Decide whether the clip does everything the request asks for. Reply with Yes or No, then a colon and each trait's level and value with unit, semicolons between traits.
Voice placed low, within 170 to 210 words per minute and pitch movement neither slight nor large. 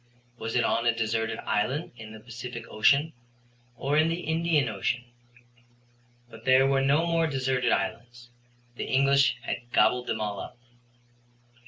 No: low, 125 Hz; average, 150 wpm; average, 3.3 semitones